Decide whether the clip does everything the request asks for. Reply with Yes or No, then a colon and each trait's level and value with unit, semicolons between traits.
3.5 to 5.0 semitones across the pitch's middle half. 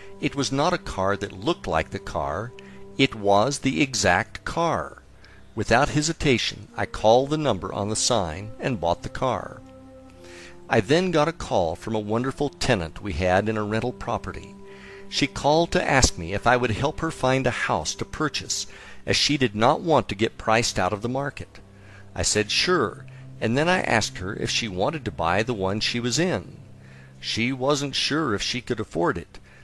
No: wide, 5.6 semitones